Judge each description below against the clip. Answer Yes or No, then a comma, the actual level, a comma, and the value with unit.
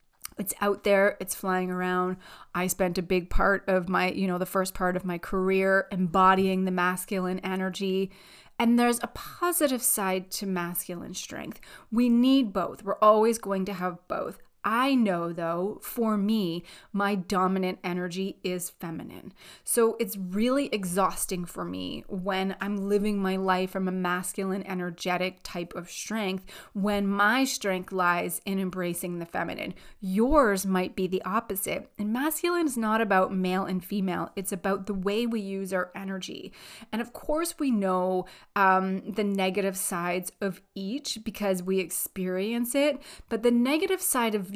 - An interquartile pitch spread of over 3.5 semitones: No, narrow, 2.6 semitones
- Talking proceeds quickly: No, average, 160 wpm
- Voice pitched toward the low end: No, high, 195 Hz